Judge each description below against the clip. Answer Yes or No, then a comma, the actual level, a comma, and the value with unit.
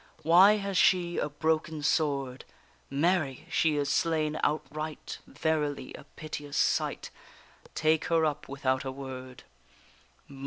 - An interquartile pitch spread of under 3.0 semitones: Yes, narrow, 2.4 semitones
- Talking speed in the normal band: No, slow, 120 wpm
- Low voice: No, medium, 150 Hz